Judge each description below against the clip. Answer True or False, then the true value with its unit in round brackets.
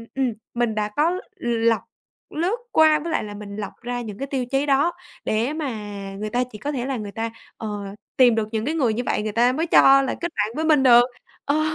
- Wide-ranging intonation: False (4.7 semitones)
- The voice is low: False (245 Hz)